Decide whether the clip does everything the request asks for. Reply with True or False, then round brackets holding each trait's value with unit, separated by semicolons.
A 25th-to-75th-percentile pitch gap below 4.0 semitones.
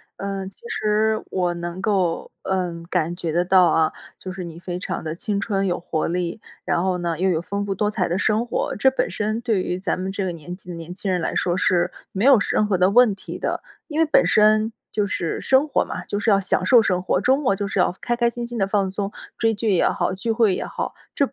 True (3.3 semitones)